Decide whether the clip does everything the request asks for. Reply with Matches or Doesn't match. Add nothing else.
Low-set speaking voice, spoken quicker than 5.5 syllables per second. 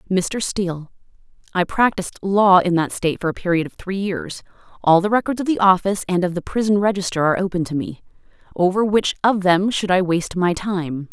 Doesn't match